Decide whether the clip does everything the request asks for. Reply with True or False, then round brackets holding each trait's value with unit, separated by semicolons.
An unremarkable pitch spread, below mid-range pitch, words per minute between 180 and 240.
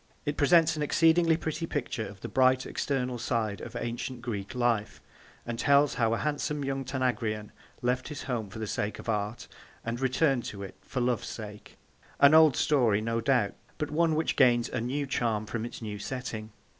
True (4.2 semitones; 125 Hz; 190 wpm)